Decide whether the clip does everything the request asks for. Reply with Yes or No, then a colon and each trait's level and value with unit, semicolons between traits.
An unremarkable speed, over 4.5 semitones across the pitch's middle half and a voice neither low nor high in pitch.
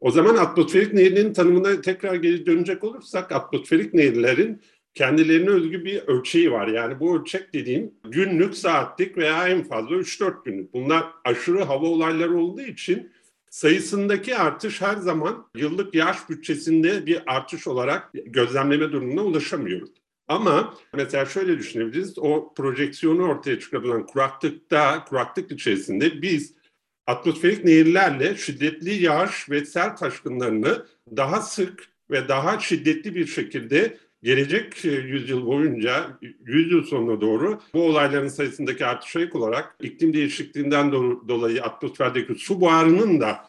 Yes: average, 125 wpm; wide, 5.4 semitones; medium, 175 Hz